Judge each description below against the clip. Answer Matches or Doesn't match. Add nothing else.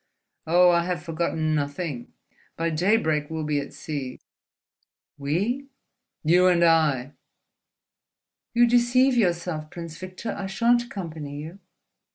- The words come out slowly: Matches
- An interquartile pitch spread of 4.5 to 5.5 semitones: Doesn't match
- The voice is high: Doesn't match